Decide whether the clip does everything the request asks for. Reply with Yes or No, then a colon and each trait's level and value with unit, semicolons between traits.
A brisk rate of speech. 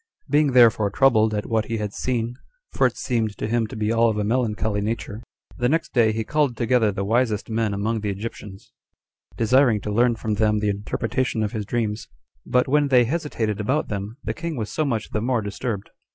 Yes: fast, 210 wpm